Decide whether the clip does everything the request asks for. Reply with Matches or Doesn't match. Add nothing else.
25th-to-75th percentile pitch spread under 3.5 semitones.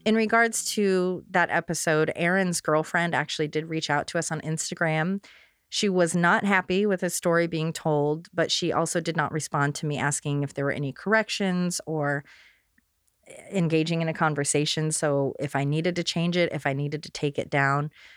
Matches